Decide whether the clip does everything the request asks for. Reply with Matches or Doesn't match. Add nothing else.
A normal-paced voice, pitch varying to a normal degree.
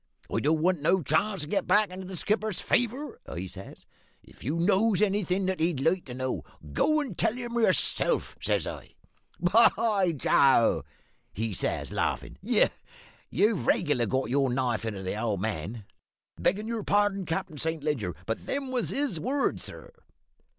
Doesn't match